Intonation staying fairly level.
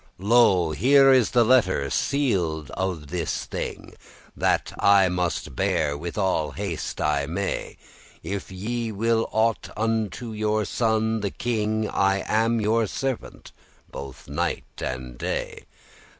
No: average, 4.6 semitones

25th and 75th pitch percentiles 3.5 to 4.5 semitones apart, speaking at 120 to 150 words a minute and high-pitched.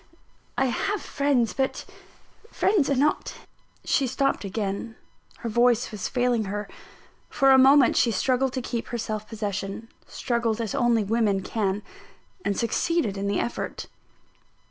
Yes: average, 4.0 semitones; average, 145 wpm; high, 235 Hz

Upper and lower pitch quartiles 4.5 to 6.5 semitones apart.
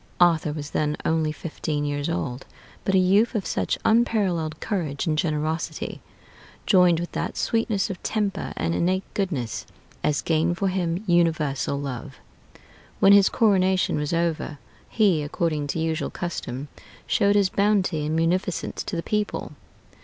No: average, 4.1 semitones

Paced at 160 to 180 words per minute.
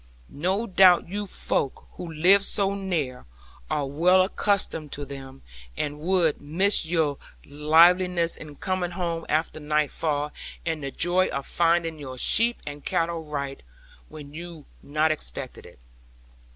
No: average, 140 wpm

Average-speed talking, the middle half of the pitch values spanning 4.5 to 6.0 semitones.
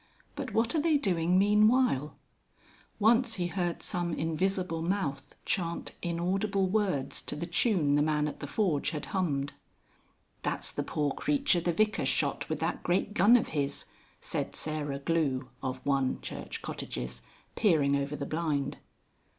Yes: average, 150 wpm; wide, 5.5 semitones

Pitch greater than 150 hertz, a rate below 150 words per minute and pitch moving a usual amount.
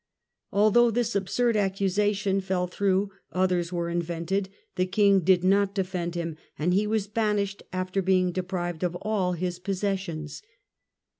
No: high, 190 Hz; average, 140 wpm; narrow, 2.1 semitones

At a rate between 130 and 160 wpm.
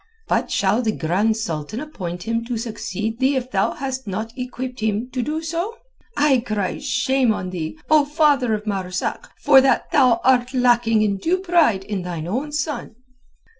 No: average, 175 wpm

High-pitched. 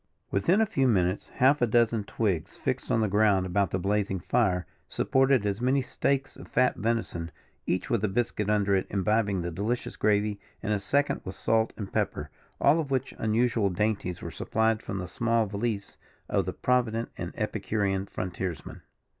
No: low, 105 Hz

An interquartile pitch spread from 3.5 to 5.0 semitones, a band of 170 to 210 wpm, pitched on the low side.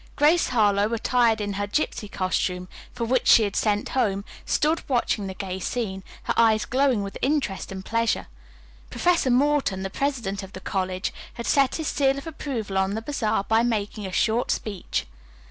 No: average, 4.7 semitones; average, 180 wpm; high, 220 Hz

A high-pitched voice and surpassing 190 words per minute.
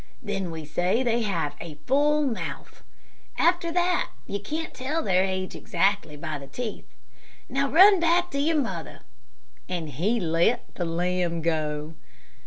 No: high, 200 Hz; average, 150 wpm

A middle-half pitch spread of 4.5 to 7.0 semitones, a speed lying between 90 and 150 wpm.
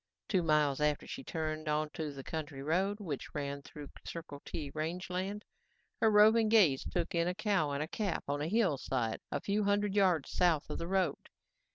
No: average, 5.1 semitones; average, 185 wpm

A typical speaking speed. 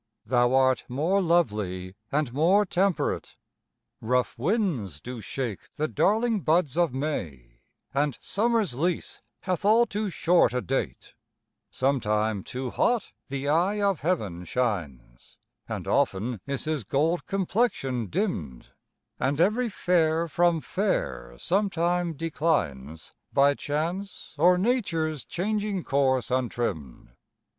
No: slow, 115 wpm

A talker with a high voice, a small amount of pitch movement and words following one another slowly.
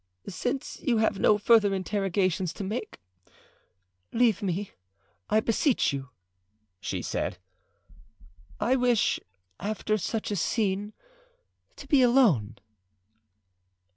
No: high, 210 Hz; average, 3.5 semitones; slow, 105 wpm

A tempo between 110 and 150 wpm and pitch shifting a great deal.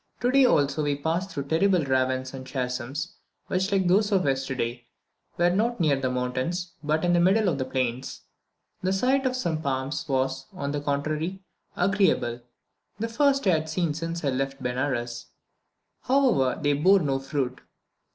No: average, 165 wpm; wide, 5.9 semitones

